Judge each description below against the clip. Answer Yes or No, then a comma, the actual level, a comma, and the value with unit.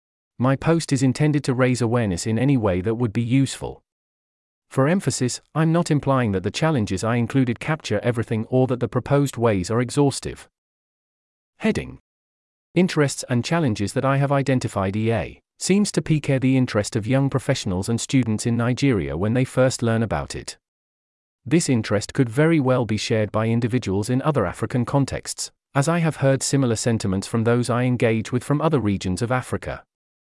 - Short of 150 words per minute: No, average, 175 wpm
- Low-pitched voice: Yes, low, 120 Hz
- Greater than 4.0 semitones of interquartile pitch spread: Yes, average, 4.6 semitones